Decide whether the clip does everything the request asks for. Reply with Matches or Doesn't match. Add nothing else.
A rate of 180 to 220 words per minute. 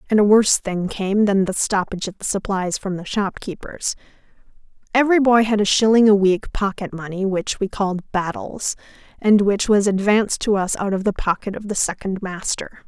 Matches